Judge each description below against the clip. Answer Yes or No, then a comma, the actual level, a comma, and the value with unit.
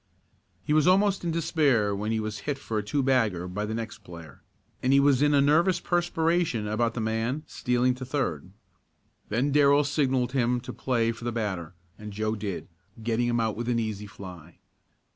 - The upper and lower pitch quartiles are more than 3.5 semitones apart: Yes, average, 4.9 semitones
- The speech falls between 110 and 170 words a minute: No, average, 195 wpm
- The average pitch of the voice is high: No, low, 120 Hz